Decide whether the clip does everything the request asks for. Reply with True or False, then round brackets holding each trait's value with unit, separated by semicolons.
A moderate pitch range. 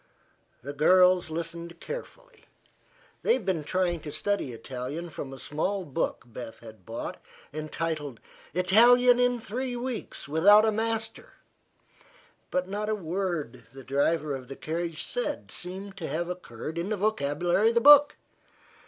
False (6.1 semitones)